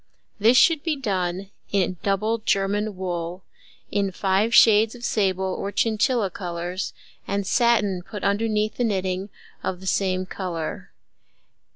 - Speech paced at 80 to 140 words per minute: Yes, slow, 135 wpm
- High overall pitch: Yes, high, 195 Hz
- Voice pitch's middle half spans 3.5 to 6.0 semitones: No, average, 2.7 semitones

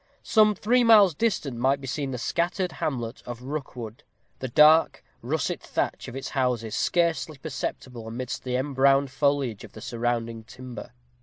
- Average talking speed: Yes, average, 155 wpm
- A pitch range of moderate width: Yes, average, 4.1 semitones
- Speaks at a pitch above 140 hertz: No, low, 135 Hz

